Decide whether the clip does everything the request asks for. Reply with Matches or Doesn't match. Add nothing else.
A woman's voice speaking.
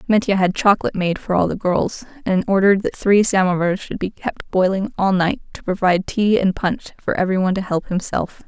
Matches